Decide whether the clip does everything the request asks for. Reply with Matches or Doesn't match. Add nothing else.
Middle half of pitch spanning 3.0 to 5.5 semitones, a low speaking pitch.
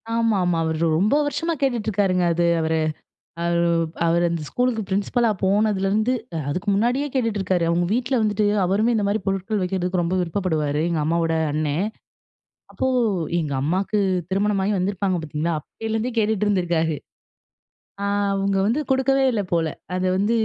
Doesn't match